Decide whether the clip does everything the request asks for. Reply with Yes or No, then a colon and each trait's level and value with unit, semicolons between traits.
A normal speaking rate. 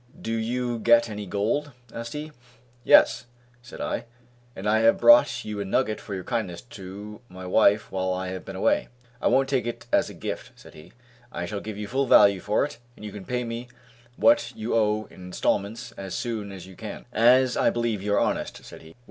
No: fast, 215 wpm